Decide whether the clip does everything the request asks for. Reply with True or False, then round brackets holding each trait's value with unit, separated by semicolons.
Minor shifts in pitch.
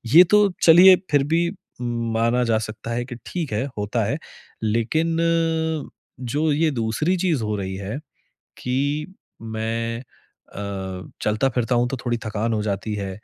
False (4.9 semitones)